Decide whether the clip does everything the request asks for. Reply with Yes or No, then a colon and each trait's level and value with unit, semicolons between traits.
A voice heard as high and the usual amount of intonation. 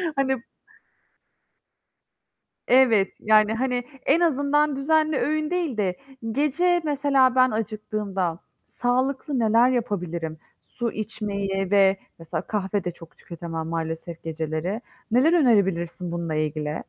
No: high, 215 Hz; wide, 7.4 semitones